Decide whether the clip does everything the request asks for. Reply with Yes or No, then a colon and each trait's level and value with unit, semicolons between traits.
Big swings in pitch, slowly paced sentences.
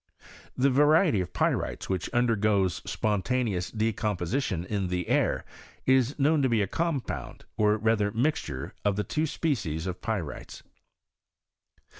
Yes: wide, 6.0 semitones; slow, 130 wpm